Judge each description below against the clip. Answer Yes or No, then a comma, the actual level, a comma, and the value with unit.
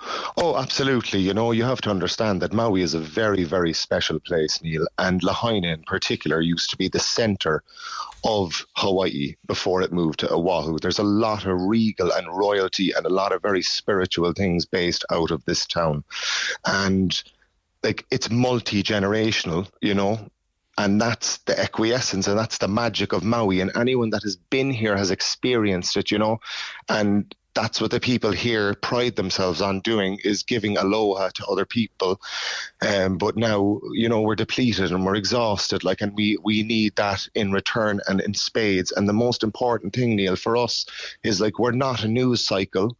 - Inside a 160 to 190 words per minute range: Yes, average, 185 wpm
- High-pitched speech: No, low, 105 Hz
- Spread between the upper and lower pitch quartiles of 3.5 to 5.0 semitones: No, average, 3.0 semitones